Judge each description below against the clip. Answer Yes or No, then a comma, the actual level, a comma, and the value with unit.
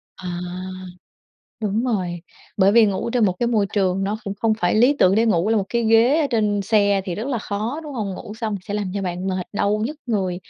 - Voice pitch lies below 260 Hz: Yes, high, 210 Hz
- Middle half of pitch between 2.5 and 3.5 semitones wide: Yes, average, 2.8 semitones